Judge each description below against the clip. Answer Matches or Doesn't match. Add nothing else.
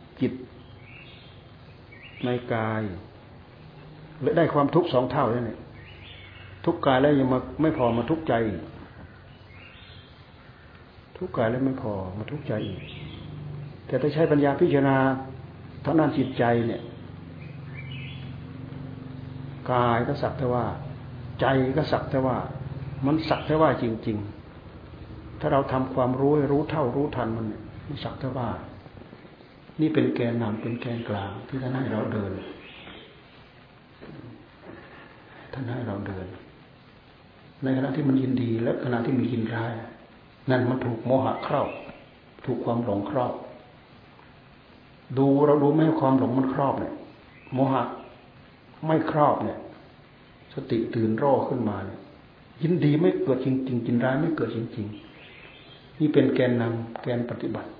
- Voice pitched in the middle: Doesn't match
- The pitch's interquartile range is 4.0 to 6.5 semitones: Doesn't match